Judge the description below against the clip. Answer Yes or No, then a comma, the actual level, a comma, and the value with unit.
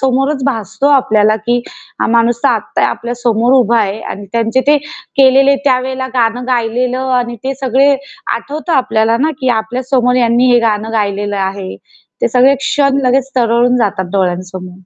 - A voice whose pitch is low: No, high, 245 Hz